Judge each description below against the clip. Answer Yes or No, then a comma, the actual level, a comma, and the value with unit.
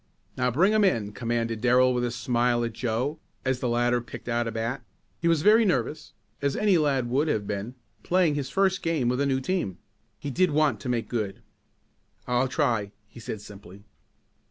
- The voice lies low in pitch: Yes, low, 125 Hz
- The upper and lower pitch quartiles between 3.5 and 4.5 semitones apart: Yes, average, 4.1 semitones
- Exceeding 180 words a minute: Yes, average, 195 wpm